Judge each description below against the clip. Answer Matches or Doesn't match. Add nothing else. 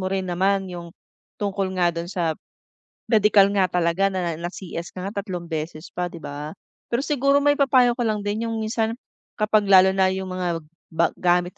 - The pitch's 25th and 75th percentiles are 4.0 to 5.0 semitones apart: Doesn't match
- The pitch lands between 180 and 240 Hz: Matches